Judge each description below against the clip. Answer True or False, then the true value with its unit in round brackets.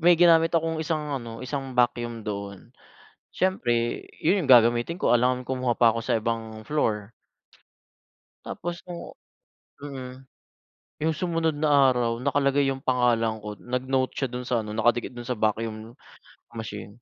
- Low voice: True (125 Hz)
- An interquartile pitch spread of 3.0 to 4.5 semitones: True (4.1 semitones)